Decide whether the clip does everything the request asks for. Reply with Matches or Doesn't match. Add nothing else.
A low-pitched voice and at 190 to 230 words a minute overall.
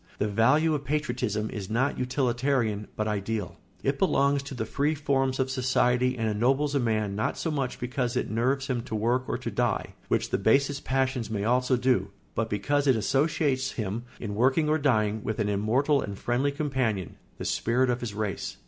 Matches